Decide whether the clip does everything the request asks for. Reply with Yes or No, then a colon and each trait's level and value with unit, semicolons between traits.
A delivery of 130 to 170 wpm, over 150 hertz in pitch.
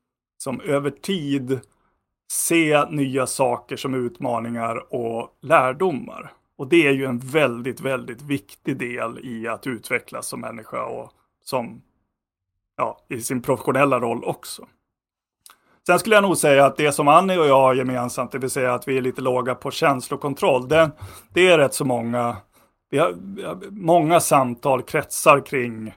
No: average, 155 wpm; low, 135 Hz